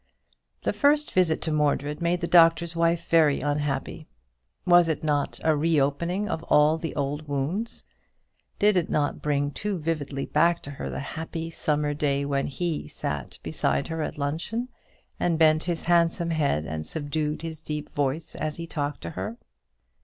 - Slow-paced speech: No, average, 170 wpm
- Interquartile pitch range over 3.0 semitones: No, average, 2.7 semitones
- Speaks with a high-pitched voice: No, medium, 155 Hz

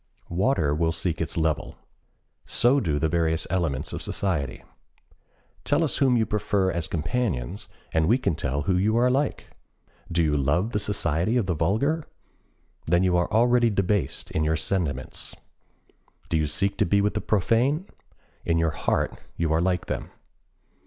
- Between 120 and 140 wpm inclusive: No, average, 165 wpm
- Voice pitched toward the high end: No, very low, 90 Hz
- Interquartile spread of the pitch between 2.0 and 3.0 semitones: No, wide, 5.4 semitones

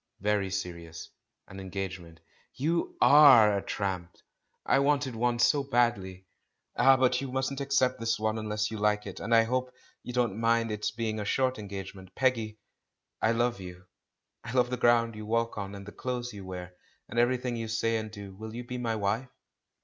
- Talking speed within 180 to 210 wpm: Yes, average, 195 wpm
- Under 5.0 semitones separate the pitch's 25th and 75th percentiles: Yes, average, 3.6 semitones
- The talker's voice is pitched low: Yes, low, 115 Hz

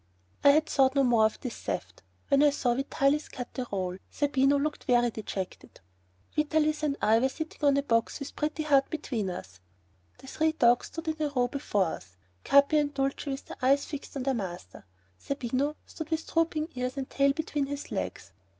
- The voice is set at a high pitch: Yes, very high, 275 Hz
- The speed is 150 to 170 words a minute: No, average, 195 wpm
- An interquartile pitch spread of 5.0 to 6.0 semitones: No, average, 3.4 semitones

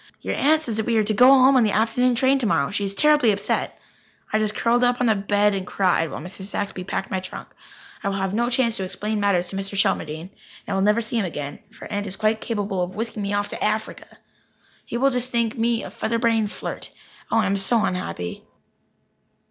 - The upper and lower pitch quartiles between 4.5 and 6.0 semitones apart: No, average, 3.3 semitones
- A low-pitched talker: No, high, 210 Hz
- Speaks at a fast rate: Yes, fast, 235 wpm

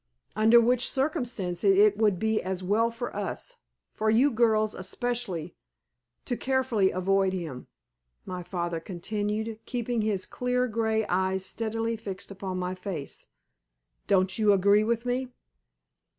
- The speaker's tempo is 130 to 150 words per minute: Yes, slow, 135 wpm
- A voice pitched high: Yes, high, 215 Hz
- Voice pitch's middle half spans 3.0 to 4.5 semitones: Yes, average, 3.6 semitones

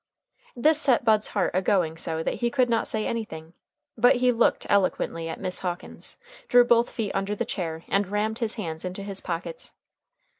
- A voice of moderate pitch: No, high, 205 Hz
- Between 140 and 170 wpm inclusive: No, average, 190 wpm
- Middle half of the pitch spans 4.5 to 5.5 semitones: Yes, average, 5.0 semitones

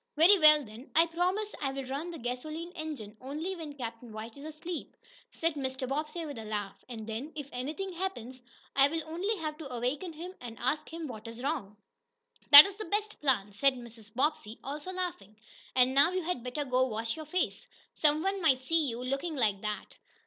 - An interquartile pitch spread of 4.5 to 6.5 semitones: Yes, average, 5.1 semitones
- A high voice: Yes, very high, 285 Hz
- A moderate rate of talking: Yes, average, 190 wpm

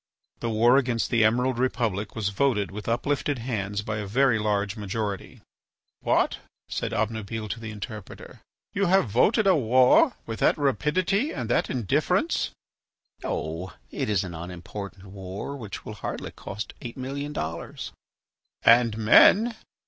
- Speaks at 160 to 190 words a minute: No, average, 145 wpm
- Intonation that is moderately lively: Yes, average, 4.3 semitones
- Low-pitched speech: Yes, low, 110 Hz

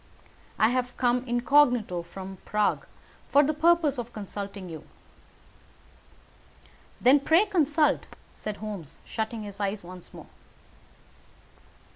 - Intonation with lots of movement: Yes, wide, 5.9 semitones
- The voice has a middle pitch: No, high, 230 Hz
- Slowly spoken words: Yes, slow, 110 wpm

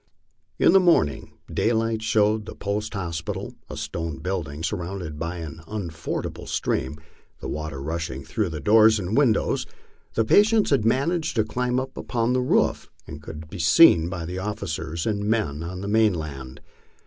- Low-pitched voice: Yes, very low, 95 Hz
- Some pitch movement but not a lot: No, wide, 5.7 semitones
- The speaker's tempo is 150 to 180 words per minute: Yes, average, 160 wpm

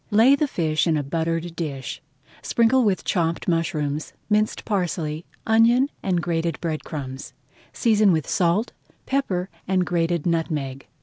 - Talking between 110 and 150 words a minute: Yes, slow, 135 wpm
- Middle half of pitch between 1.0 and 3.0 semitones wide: No, average, 4.9 semitones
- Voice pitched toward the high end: No, medium, 170 Hz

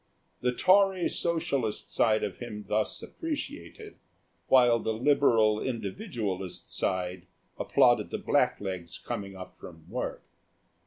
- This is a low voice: Yes, low, 110 Hz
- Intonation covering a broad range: Yes, wide, 6.0 semitones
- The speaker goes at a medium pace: No, slow, 110 wpm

